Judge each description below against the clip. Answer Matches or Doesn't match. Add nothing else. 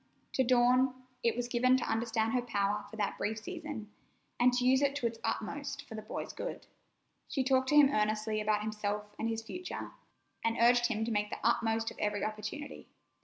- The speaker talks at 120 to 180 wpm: Doesn't match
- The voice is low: Doesn't match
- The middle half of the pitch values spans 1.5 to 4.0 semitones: Matches